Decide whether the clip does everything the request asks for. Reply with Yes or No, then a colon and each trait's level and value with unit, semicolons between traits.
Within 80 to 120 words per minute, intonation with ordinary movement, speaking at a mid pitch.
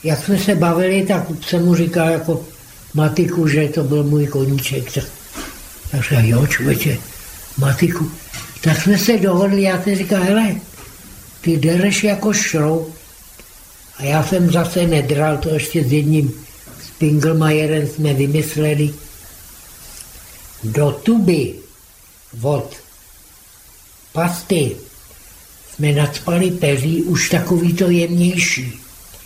Yes: slow, 115 wpm; average, 4.0 semitones; medium, 155 Hz